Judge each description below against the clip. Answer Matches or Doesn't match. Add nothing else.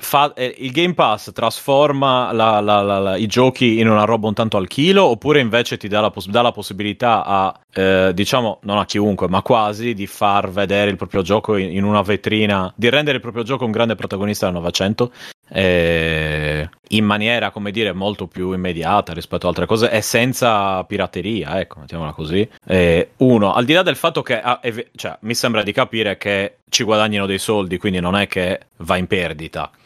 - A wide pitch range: Doesn't match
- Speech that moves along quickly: Matches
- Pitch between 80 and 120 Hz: Matches